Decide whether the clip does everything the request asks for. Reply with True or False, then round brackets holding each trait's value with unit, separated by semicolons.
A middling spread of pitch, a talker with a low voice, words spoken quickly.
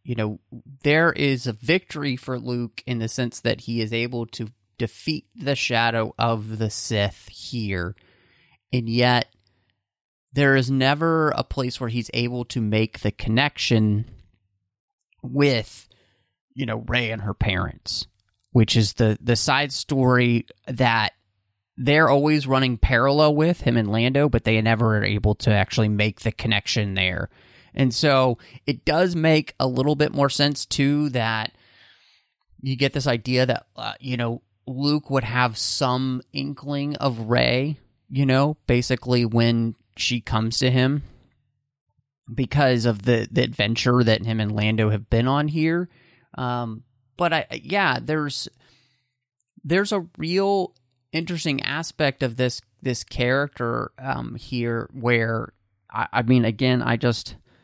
False (3.7 semitones; 125 Hz; 145 wpm)